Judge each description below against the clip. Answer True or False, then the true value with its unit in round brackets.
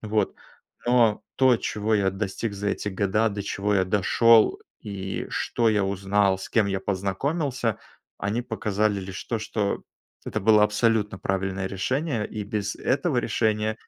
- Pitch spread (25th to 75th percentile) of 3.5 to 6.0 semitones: False (2.4 semitones)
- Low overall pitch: True (105 Hz)